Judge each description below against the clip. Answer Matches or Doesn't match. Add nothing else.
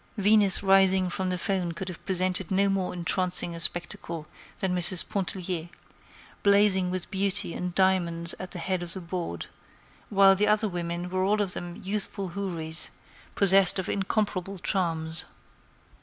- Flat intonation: Matches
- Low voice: Doesn't match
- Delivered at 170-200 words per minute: Doesn't match